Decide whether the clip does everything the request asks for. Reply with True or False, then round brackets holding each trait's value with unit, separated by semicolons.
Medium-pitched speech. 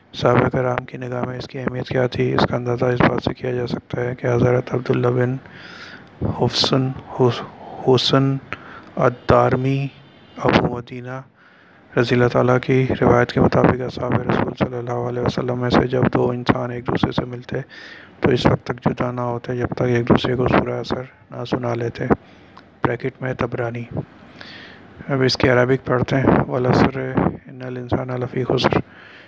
False (125 Hz)